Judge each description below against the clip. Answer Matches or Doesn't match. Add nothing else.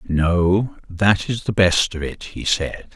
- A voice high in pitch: Doesn't match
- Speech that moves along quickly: Doesn't match